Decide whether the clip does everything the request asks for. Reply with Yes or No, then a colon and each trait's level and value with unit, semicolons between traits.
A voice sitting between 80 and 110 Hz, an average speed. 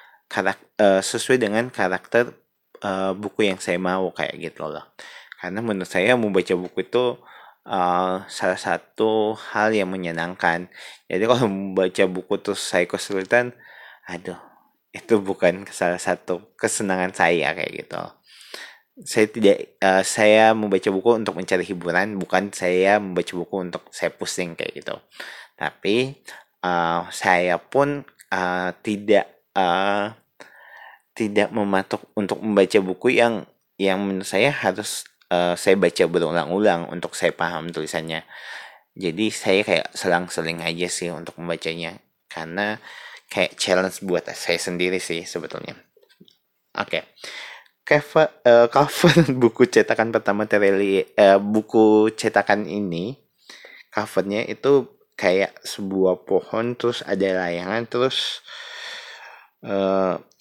Yes: low, 100 Hz; average, 120 wpm